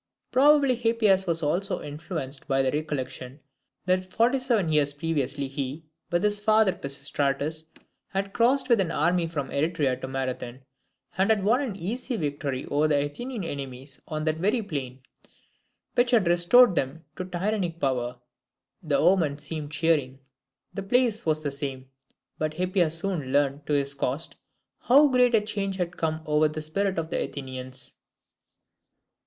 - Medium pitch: Yes, medium, 160 Hz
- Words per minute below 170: Yes, average, 155 wpm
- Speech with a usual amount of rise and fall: No, wide, 5.8 semitones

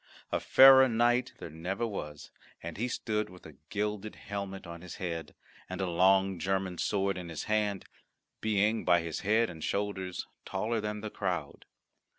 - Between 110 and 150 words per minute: No, average, 165 wpm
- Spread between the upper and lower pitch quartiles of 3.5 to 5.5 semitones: No, average, 3.1 semitones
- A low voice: Yes, very low, 95 Hz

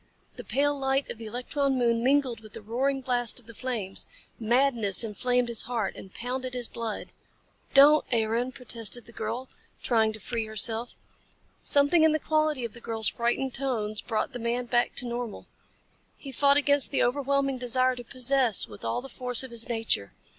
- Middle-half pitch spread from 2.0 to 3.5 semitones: Yes, average, 2.9 semitones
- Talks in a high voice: Yes, high, 245 Hz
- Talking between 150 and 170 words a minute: No, average, 185 wpm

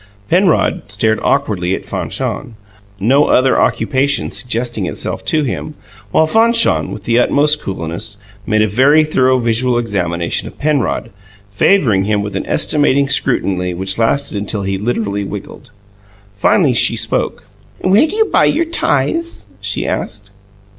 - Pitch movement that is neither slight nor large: No, wide, 6.4 semitones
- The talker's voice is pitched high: No, low, 120 Hz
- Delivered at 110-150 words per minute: Yes, average, 140 wpm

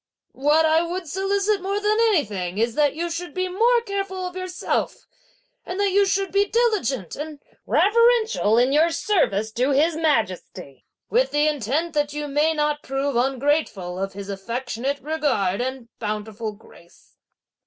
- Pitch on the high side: Yes, very high, 300 Hz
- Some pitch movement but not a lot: No, wide, 7.9 semitones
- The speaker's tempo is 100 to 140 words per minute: No, average, 155 wpm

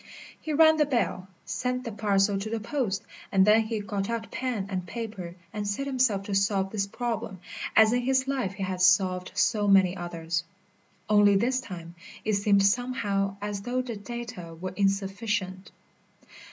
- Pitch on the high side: Yes, high, 205 Hz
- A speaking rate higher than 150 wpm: Yes, average, 170 wpm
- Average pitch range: Yes, average, 3.4 semitones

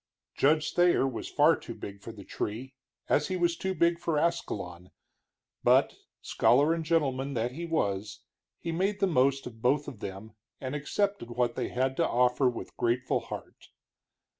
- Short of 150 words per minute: No, average, 170 wpm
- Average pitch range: No, wide, 5.8 semitones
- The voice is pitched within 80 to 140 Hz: Yes, low, 135 Hz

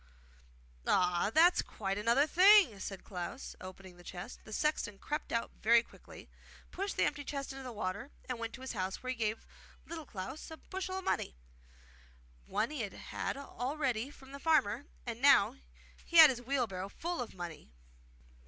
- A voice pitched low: No, high, 245 Hz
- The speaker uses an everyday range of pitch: No, wide, 6.4 semitones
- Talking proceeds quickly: No, average, 180 wpm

